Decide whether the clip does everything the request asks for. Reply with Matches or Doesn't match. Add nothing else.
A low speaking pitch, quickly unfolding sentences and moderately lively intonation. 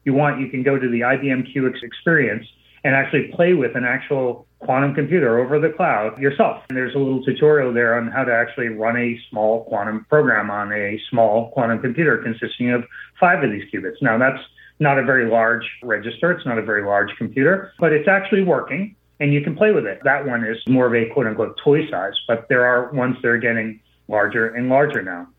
Matches